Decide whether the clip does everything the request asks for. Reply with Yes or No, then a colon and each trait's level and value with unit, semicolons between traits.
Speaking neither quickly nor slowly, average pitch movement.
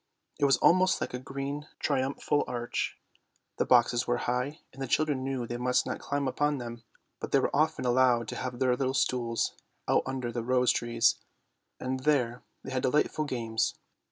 No: average, 190 wpm; narrow, 2.2 semitones